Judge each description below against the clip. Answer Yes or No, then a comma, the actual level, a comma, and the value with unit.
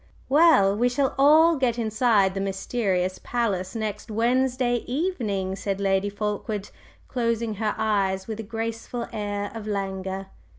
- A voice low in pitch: No, high, 215 Hz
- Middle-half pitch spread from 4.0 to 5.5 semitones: No, average, 3.6 semitones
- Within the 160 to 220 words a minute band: No, slow, 135 wpm